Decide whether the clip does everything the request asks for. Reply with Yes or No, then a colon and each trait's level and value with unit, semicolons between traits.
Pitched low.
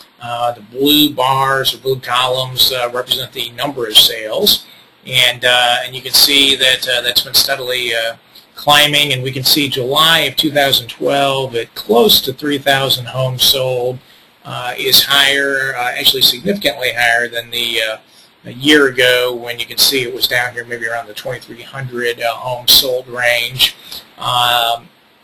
Yes: low, 125 Hz